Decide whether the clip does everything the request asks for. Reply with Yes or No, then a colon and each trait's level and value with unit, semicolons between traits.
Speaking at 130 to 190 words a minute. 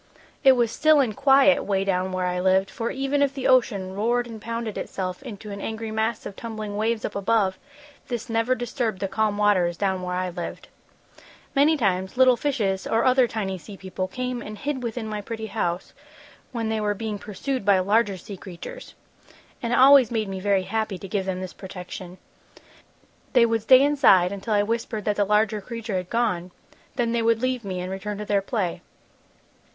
No: average, 200 wpm